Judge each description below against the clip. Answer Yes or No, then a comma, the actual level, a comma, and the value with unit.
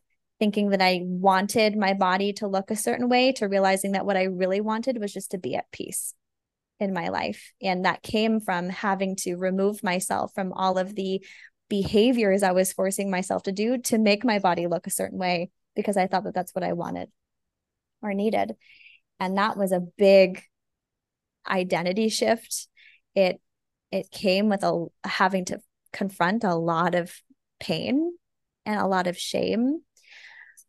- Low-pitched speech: No, high, 195 Hz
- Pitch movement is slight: Yes, narrow, 2.2 semitones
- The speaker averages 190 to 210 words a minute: No, average, 170 wpm